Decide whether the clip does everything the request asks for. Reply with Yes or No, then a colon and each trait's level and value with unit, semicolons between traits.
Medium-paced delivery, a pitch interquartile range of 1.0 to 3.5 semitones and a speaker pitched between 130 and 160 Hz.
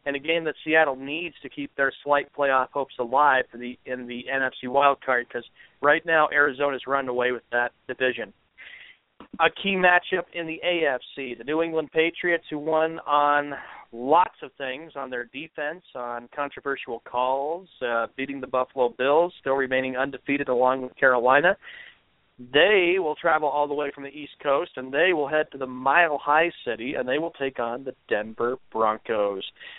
Yes: average, 175 wpm; average, 3.2 semitones; medium, 140 Hz